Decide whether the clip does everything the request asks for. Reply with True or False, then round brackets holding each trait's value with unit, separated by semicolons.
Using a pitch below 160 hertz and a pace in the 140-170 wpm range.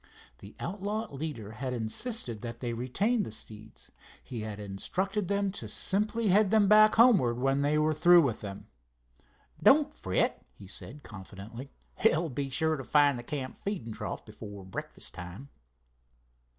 True (140 Hz; 160 wpm)